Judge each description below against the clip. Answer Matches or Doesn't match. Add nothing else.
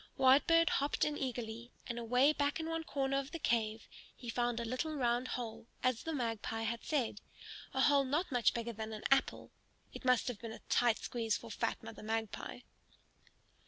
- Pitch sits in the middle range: Doesn't match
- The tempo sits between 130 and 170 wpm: Doesn't match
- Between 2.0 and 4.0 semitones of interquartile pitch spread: Matches